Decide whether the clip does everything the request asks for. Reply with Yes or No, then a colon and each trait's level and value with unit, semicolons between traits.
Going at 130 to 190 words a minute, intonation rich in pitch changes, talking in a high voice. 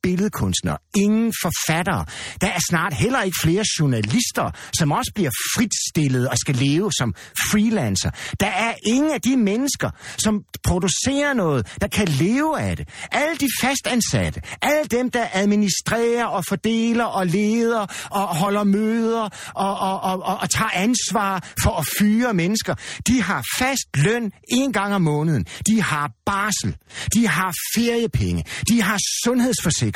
Yes: average, 150 wpm; wide, 6.0 semitones; high, 200 Hz